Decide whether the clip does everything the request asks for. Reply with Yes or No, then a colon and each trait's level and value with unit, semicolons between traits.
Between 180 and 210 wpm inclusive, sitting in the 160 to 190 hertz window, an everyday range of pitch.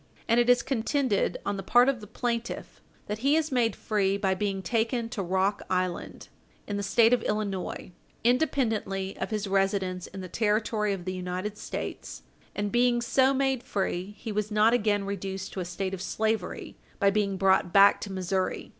No: average, 185 wpm; high, 205 Hz; average, 3.3 semitones